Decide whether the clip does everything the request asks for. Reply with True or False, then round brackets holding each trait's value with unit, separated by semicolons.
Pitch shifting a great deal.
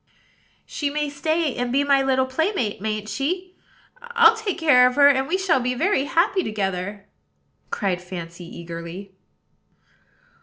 True (8.2 semitones)